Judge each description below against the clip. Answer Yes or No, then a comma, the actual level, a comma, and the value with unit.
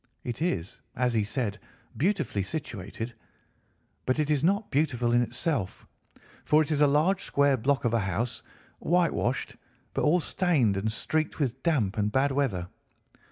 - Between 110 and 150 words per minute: No, average, 160 wpm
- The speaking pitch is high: No, low, 130 Hz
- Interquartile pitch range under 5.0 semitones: No, wide, 5.6 semitones